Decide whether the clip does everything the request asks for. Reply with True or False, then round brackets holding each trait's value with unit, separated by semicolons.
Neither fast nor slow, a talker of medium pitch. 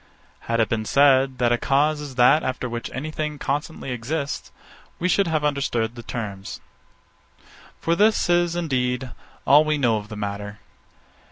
False (170 wpm; 130 Hz)